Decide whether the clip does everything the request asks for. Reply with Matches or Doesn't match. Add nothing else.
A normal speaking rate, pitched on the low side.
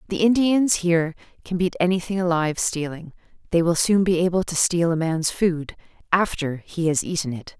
Doesn't match